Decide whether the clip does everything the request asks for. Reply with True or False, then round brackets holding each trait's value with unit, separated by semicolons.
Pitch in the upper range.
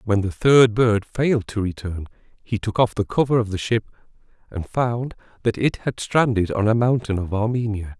False (110 Hz)